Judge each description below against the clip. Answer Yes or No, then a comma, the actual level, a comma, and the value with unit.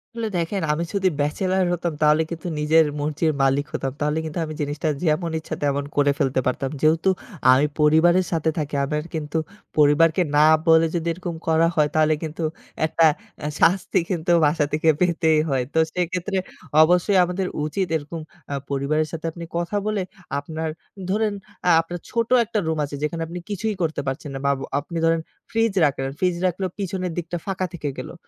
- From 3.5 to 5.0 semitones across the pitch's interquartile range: No, average, 3.0 semitones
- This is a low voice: No, medium, 160 Hz